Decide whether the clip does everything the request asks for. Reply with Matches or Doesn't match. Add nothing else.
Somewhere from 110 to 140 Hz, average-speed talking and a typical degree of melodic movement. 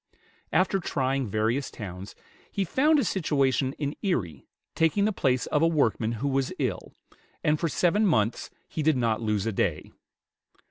Doesn't match